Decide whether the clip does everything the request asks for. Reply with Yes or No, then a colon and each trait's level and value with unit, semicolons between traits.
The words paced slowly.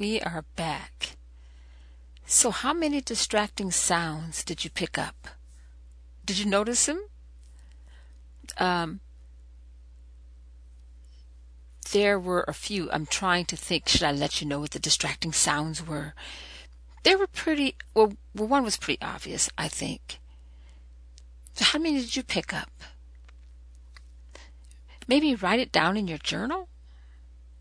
Yes: slow, 130 wpm